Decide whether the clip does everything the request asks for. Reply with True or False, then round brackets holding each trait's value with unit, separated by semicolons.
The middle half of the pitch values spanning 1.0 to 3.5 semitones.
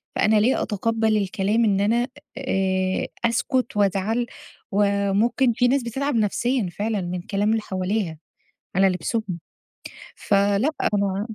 True (3.1 semitones)